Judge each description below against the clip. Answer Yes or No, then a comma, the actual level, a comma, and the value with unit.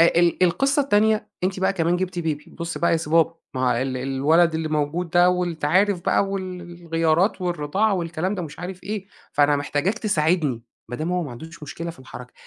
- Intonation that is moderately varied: Yes, average, 3.5 semitones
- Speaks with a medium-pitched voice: Yes, medium, 170 Hz